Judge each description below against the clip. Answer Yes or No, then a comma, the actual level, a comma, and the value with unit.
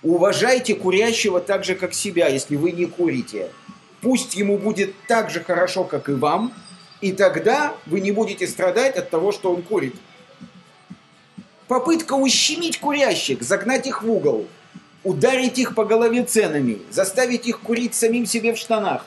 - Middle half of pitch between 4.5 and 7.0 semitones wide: Yes, average, 5.0 semitones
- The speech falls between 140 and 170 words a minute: Yes, average, 155 wpm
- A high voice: Yes, high, 220 Hz